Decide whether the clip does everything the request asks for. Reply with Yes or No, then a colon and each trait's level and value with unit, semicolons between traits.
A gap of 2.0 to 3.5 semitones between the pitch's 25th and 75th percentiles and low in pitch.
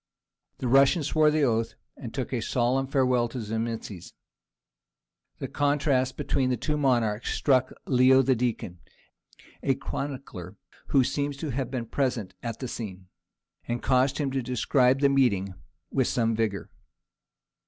Yes: average, 3.0 semitones; low, 125 Hz